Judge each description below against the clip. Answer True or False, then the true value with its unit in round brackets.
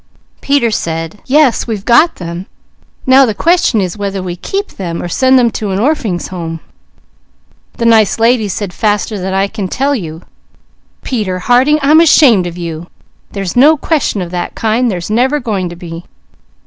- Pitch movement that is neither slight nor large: False (6.1 semitones)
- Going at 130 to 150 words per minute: False (175 wpm)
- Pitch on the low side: False (210 Hz)